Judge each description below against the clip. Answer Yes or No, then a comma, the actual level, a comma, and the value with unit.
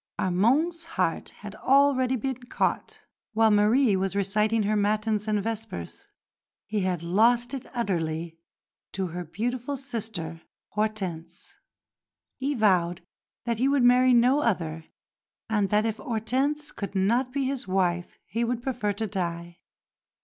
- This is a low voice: No, high, 215 Hz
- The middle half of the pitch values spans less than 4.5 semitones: No, average, 4.8 semitones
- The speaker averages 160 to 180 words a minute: No, slow, 135 wpm